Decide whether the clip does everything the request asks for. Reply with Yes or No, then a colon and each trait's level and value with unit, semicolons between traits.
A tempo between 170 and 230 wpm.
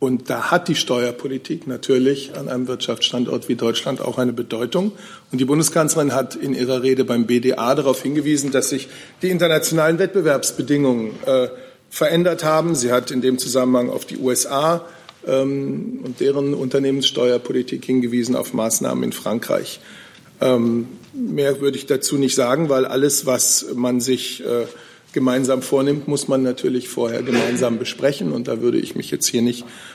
No: average, 160 wpm